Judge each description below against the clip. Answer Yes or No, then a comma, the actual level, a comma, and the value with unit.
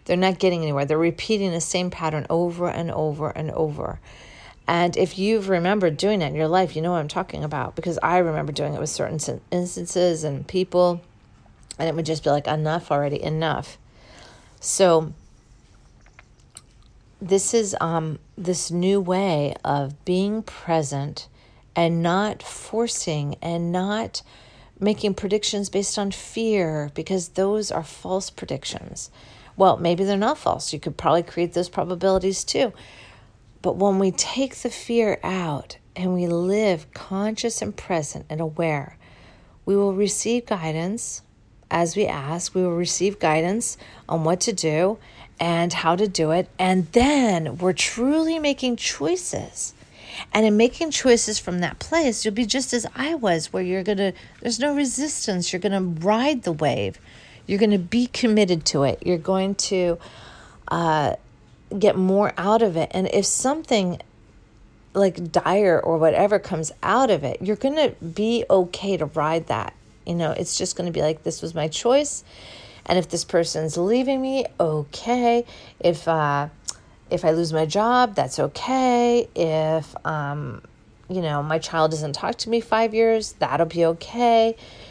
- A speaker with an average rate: Yes, average, 165 wpm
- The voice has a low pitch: No, medium, 180 Hz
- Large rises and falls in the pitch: No, average, 4.8 semitones